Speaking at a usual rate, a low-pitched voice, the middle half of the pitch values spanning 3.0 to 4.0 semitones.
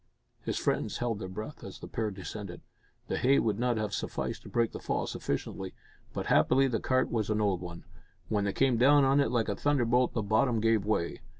No: fast, 215 wpm; low, 110 Hz; average, 3.6 semitones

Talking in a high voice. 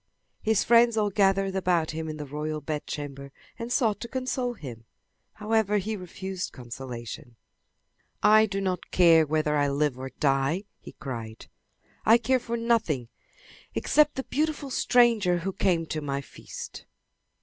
No: medium, 180 Hz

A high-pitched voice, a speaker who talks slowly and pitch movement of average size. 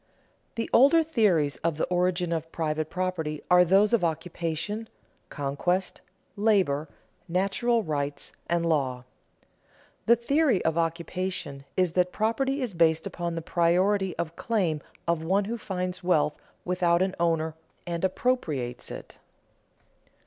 No: medium, 175 Hz; slow, 130 wpm; average, 3.5 semitones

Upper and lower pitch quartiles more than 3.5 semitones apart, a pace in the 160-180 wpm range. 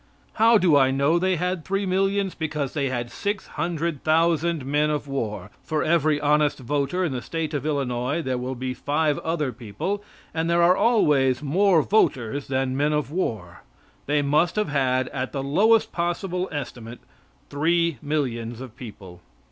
Yes: average, 4.5 semitones; average, 170 wpm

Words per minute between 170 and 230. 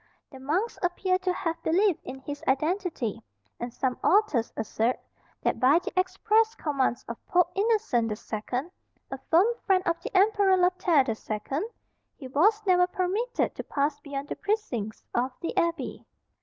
No: average, 160 wpm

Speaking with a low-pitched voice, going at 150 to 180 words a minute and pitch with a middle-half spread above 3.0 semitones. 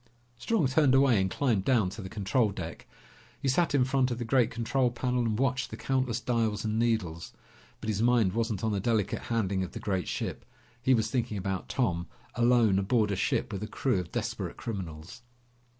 No: low, 115 Hz; average, 200 wpm; average, 4.3 semitones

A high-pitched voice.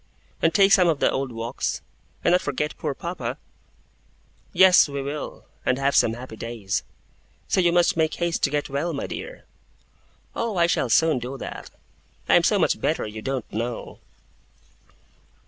No: medium, 145 Hz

